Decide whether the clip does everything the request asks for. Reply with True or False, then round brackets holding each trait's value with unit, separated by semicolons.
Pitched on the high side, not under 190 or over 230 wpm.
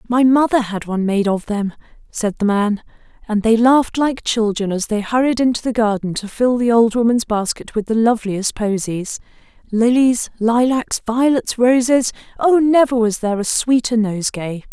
False (230 Hz; 165 wpm)